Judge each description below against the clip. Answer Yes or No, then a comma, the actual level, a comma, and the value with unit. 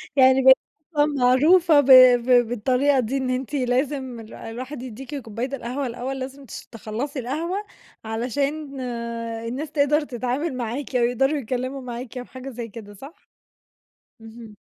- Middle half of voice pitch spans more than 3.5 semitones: No, narrow, 2.6 semitones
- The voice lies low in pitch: No, very high, 260 Hz